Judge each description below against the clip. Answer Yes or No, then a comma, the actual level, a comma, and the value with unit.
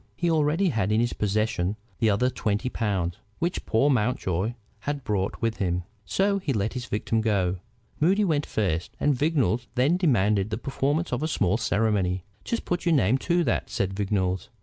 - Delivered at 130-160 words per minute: No, average, 180 wpm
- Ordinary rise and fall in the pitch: No, wide, 6.6 semitones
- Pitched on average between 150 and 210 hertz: No, low, 115 Hz